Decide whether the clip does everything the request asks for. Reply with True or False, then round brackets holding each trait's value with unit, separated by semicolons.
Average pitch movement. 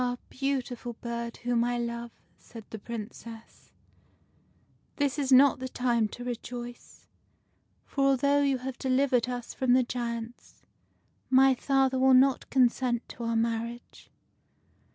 False (2.0 semitones)